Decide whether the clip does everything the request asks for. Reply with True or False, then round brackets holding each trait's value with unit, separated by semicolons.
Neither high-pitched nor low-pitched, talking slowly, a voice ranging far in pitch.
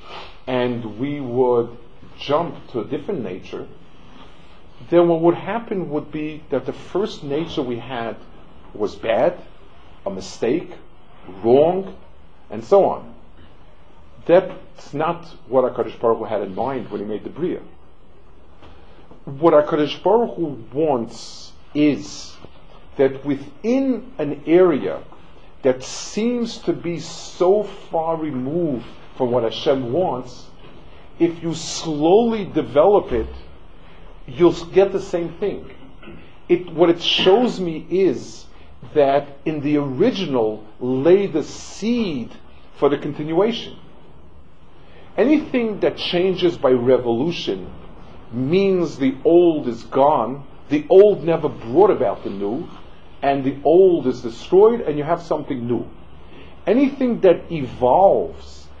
True (150 Hz; 120 wpm; 7.2 semitones)